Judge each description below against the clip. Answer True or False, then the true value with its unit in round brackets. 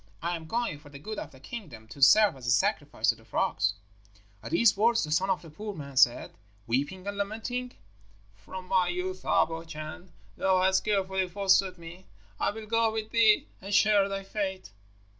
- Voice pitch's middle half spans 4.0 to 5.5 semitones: True (4.7 semitones)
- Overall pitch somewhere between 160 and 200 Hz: True (190 Hz)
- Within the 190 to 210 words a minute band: True (195 wpm)